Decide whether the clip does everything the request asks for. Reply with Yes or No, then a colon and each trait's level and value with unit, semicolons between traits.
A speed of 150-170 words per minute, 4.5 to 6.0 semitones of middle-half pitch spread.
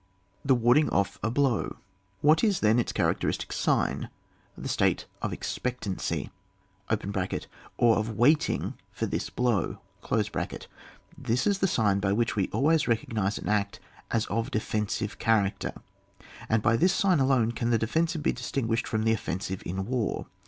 No: average, 160 wpm; average, 3.9 semitones